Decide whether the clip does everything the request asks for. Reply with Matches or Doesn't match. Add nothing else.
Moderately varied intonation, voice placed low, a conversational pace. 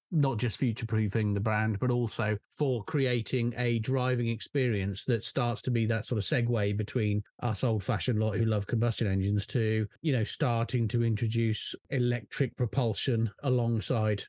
Doesn't match